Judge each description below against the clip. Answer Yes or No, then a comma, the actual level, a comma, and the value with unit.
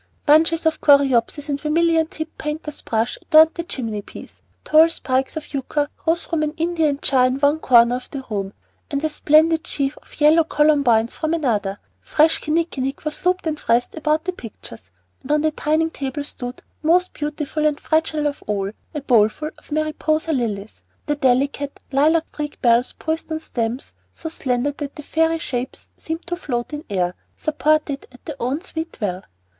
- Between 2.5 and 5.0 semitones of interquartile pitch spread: Yes, average, 3.7 semitones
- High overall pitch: Yes, very high, 295 Hz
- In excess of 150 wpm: Yes, average, 175 wpm